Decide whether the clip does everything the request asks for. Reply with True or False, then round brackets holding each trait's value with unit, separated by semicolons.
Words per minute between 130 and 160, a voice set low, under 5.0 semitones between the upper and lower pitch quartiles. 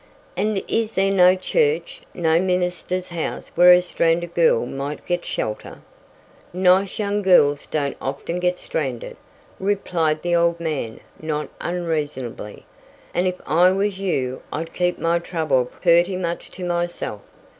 False (140 wpm; 175 Hz; 2.9 semitones)